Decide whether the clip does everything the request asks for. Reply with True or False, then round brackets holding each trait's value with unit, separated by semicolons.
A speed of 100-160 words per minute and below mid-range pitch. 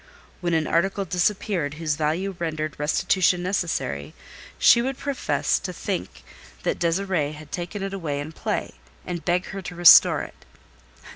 False (150 wpm; 175 Hz)